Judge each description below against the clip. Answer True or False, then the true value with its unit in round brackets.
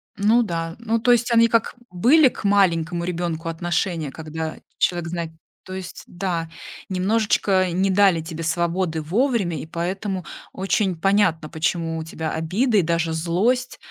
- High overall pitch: False (180 Hz)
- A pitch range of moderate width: True (3.6 semitones)